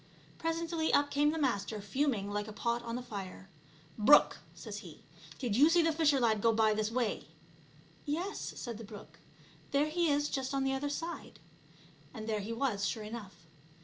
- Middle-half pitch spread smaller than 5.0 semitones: No, wide, 5.6 semitones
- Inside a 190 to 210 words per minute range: Yes, average, 195 wpm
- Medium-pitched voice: No, high, 240 Hz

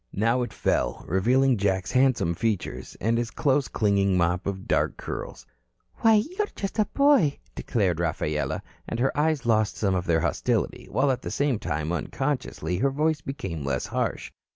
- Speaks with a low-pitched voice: Yes, low, 115 Hz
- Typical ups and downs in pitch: No, wide, 7.2 semitones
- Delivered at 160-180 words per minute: Yes, average, 175 wpm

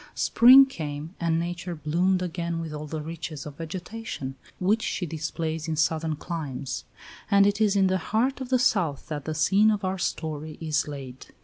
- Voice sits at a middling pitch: Yes, medium, 165 Hz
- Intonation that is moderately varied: Yes, average, 4.0 semitones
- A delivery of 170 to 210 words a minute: Yes, average, 185 wpm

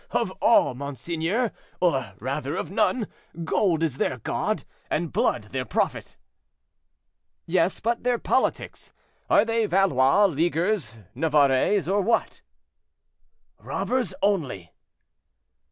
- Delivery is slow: Yes, slow, 105 wpm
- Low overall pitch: No, medium, 170 Hz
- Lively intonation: Yes, wide, 6.7 semitones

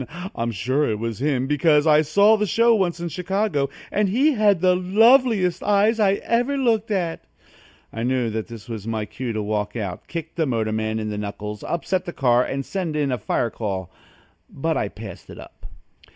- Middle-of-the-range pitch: Yes, medium, 150 Hz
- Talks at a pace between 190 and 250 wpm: Yes, average, 195 wpm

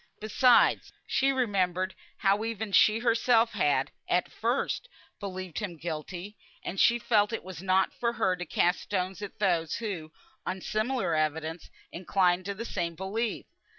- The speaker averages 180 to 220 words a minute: No, average, 150 wpm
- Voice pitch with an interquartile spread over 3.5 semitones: Yes, average, 4.1 semitones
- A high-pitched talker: Yes, high, 195 Hz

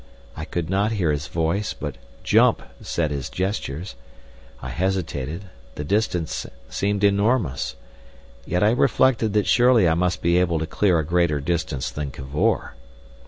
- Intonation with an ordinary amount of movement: Yes, average, 4.9 semitones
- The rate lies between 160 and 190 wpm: No, average, 150 wpm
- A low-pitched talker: Yes, very low, 85 Hz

